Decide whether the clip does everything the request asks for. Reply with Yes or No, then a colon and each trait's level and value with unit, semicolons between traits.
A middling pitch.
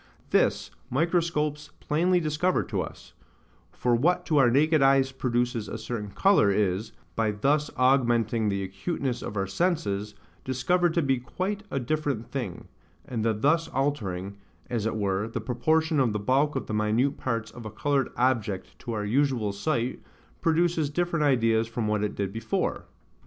No: low, 125 Hz